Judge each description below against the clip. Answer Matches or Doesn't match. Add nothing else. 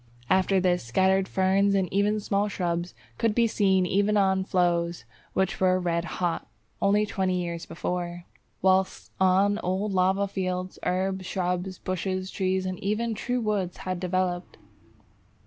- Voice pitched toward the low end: Doesn't match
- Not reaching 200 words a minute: Matches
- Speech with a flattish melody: Matches